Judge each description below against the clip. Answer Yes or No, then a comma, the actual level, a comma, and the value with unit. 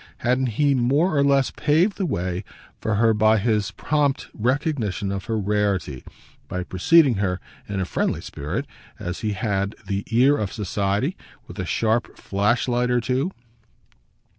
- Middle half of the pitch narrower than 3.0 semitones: No, average, 5.3 semitones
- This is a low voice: Yes, low, 110 Hz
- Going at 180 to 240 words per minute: No, average, 155 wpm